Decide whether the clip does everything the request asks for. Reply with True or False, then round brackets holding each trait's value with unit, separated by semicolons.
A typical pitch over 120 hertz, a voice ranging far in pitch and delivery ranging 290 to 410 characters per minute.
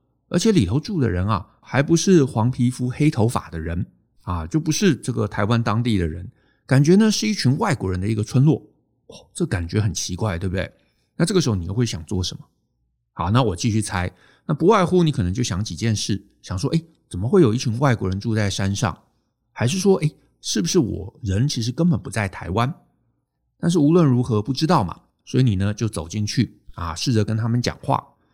False (115 Hz; 6.0 semitones; 305 characters per minute)